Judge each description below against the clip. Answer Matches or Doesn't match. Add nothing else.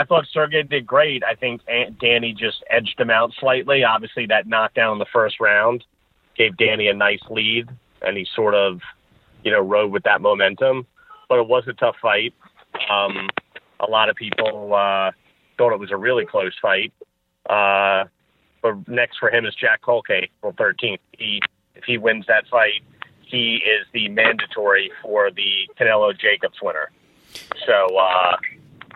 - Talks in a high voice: Doesn't match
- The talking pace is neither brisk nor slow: Matches